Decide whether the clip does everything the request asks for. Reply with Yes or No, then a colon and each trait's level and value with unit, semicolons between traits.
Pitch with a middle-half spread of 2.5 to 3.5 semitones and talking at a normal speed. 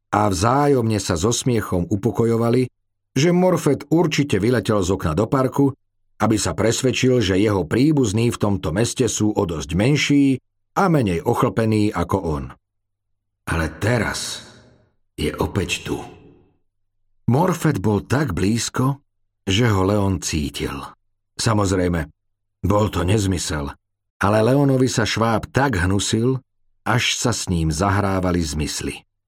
No: average, 4.0 semitones; average, 125 wpm